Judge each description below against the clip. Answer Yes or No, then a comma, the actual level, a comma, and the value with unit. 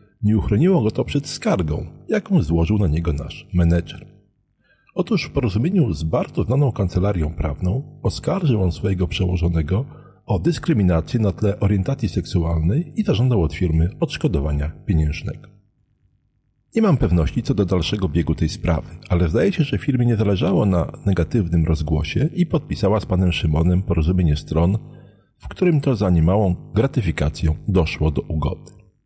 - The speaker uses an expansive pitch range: Yes, wide, 6.6 semitones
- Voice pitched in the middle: No, very low, 95 Hz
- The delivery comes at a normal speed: Yes, average, 145 wpm